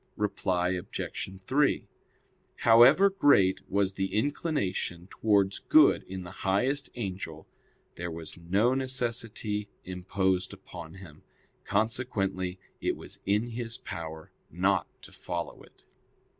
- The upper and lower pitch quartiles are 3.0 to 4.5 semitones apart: Yes, average, 4.2 semitones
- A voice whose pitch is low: Yes, very low, 95 Hz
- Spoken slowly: Yes, slow, 115 wpm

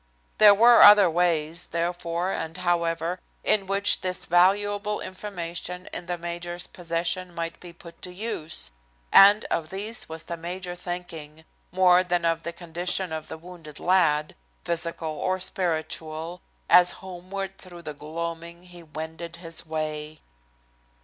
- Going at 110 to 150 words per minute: Yes, average, 140 wpm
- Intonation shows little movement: Yes, narrow, 1.8 semitones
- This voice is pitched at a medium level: Yes, medium, 175 Hz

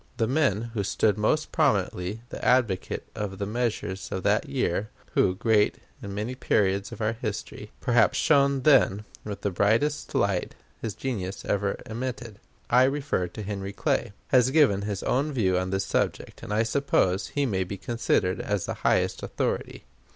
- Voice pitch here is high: No, low, 105 Hz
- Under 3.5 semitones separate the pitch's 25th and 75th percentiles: No, average, 4.2 semitones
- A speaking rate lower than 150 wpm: No, average, 170 wpm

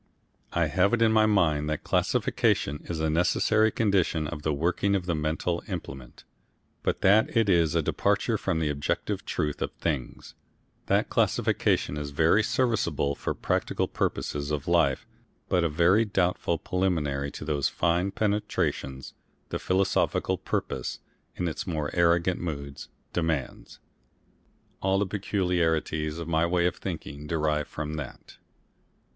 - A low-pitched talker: Yes, very low, 85 Hz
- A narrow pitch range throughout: No, average, 3.7 semitones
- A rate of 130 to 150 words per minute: Yes, average, 145 wpm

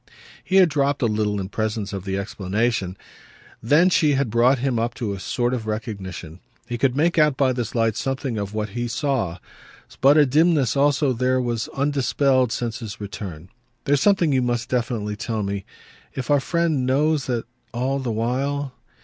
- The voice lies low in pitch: Yes, low, 125 Hz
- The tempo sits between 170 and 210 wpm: Yes, average, 185 wpm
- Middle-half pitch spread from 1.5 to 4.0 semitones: No, average, 4.4 semitones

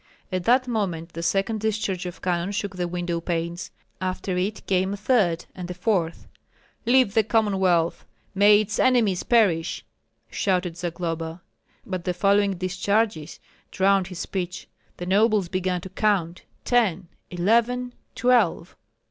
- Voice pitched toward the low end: No, high, 190 Hz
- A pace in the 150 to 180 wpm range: No, average, 140 wpm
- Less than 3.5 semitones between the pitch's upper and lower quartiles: Yes, average, 3.1 semitones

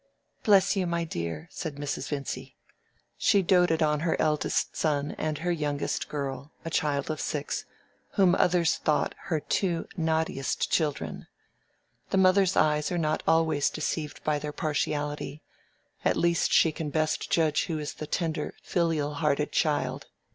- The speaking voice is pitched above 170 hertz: No, medium, 155 Hz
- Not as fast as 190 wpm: Yes, average, 150 wpm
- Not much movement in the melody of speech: Yes, narrow, 2.3 semitones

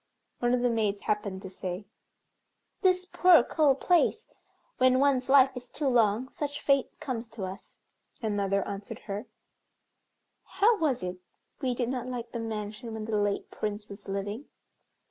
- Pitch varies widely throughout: No, average, 4.4 semitones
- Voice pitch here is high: Yes, high, 235 Hz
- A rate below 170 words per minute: Yes, average, 160 wpm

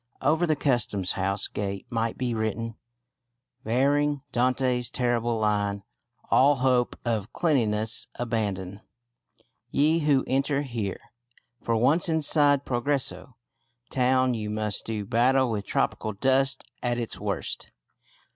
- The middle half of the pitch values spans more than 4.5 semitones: No, average, 3.8 semitones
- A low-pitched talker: Yes, low, 120 Hz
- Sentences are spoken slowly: Yes, slow, 120 wpm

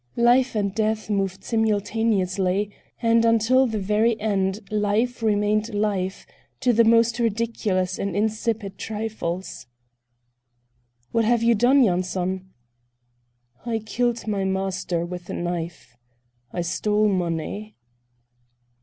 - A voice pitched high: Yes, high, 210 Hz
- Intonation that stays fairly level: No, average, 3.2 semitones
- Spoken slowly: Yes, slow, 110 wpm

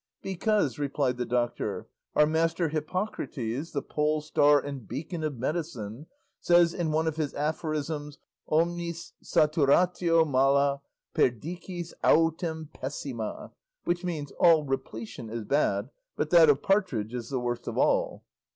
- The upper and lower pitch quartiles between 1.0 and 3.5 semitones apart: No, average, 3.9 semitones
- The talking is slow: Yes, slow, 130 wpm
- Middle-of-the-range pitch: Yes, medium, 150 Hz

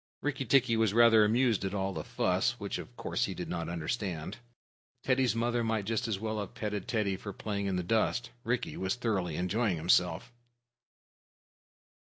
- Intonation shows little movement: No, average, 3.7 semitones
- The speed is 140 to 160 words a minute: No, average, 175 wpm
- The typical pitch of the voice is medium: No, low, 105 Hz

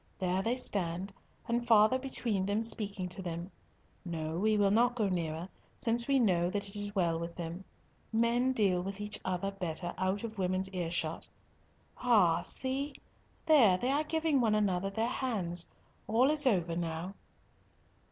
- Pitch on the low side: No, high, 200 Hz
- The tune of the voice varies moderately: Yes, average, 4.7 semitones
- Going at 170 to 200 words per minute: No, average, 160 wpm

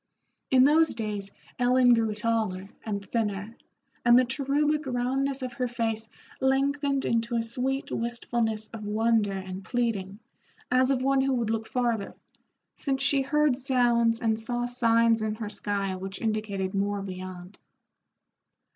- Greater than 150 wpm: No, average, 145 wpm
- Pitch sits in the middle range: No, high, 230 Hz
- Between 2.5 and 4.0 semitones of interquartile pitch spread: Yes, average, 3.5 semitones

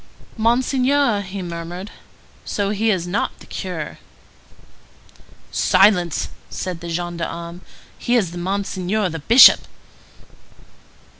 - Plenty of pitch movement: No, average, 3.8 semitones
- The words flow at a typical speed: No, slow, 95 wpm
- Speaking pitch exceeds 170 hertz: Yes, high, 190 Hz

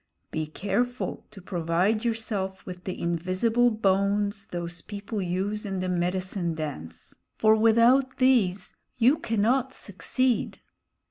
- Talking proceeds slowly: Yes, slow, 120 wpm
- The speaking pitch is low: No, high, 200 Hz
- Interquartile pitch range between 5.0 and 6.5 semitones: No, average, 3.9 semitones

